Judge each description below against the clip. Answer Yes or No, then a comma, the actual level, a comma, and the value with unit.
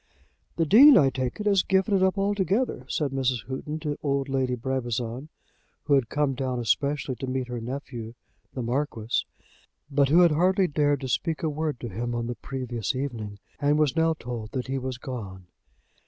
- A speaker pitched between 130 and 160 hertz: Yes, low, 135 Hz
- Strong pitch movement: No, average, 3.8 semitones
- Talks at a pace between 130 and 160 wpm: No, average, 190 wpm